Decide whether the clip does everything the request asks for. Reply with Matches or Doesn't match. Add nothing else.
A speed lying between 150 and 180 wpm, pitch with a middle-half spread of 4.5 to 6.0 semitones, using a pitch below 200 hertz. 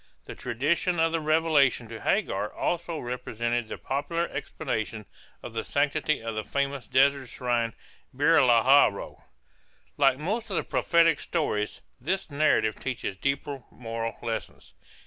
Doesn't match